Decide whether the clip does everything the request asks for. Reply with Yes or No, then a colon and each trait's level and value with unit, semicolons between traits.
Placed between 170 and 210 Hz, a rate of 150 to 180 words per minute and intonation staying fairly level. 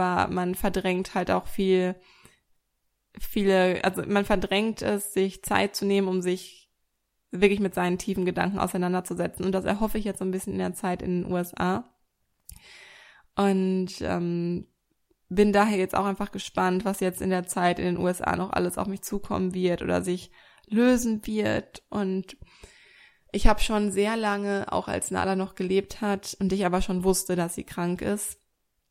Yes: high, 190 Hz; average, 175 wpm; narrow, 1.9 semitones